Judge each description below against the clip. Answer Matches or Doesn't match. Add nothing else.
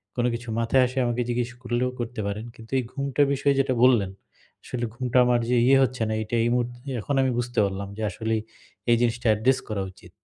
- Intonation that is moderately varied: Doesn't match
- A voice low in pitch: Matches